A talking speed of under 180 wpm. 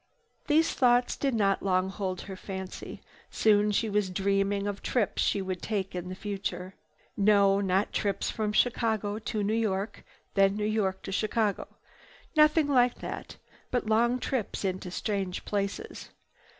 Yes: average, 150 wpm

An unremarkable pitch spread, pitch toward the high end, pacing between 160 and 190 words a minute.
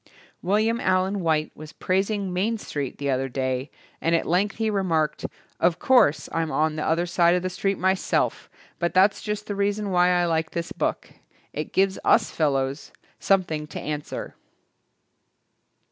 No: average, 4.1 semitones; medium, 175 Hz; average, 165 wpm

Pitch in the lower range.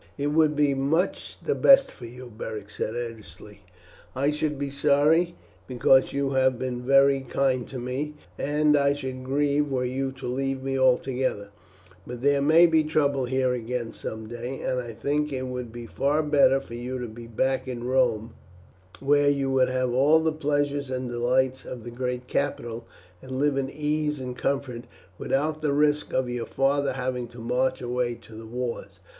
Yes: low, 130 Hz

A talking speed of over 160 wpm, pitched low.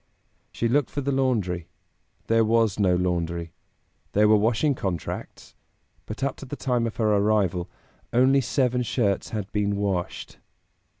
No: average, 145 wpm; low, 110 Hz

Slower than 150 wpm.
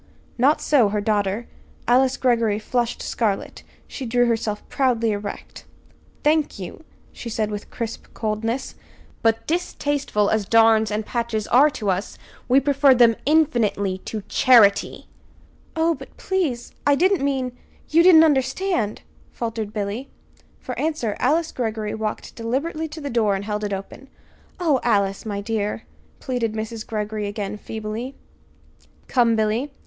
Yes: average, 140 wpm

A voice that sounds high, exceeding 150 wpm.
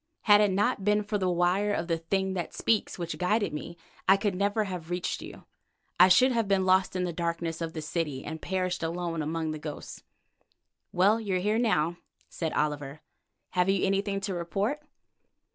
No: medium, 180 Hz; average, 195 wpm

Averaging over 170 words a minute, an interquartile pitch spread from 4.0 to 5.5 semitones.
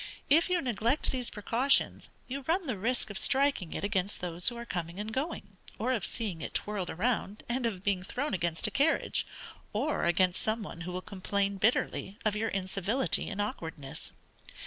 Yes: average, 185 wpm; average, 5.1 semitones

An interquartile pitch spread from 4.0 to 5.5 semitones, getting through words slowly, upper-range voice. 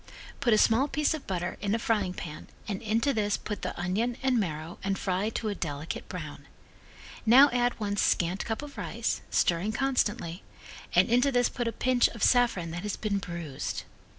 No: average, 4.9 semitones; average, 190 wpm; high, 215 Hz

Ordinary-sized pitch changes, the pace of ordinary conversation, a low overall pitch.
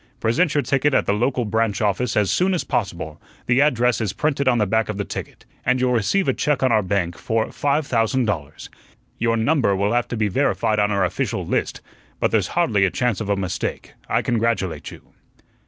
No: average, 4.1 semitones; fast, 215 wpm; low, 115 Hz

